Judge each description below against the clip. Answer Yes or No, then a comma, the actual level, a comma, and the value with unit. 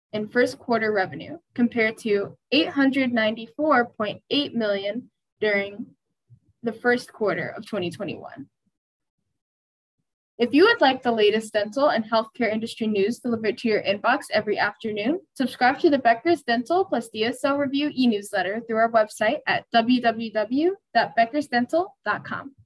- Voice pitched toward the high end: Yes, high, 230 Hz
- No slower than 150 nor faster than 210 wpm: No, average, 140 wpm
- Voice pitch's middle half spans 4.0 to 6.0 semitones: Yes, average, 4.3 semitones